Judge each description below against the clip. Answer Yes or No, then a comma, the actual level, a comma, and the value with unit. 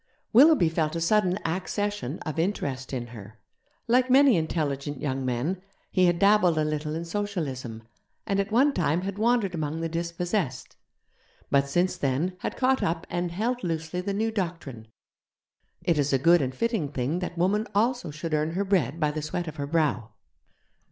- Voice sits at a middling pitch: Yes, medium, 170 Hz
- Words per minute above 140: Yes, average, 180 wpm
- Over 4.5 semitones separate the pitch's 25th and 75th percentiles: Yes, average, 5.1 semitones